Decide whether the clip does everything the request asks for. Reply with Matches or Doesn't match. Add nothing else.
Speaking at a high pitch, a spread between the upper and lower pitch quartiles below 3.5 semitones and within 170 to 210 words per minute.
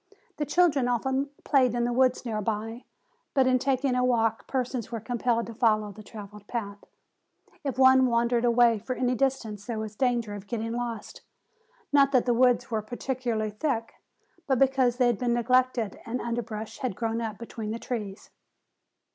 Matches